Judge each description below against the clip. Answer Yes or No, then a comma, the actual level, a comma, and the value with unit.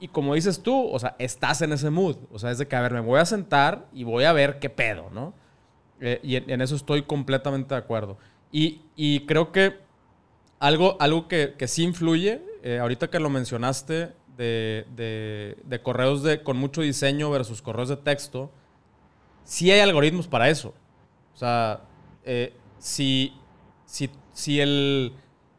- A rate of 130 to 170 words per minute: No, average, 180 wpm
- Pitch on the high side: No, medium, 140 Hz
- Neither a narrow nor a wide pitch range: Yes, average, 4.0 semitones